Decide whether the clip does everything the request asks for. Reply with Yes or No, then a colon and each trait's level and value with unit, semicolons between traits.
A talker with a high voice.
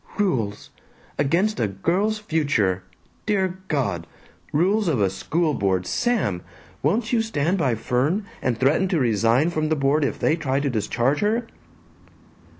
No: medium, 150 Hz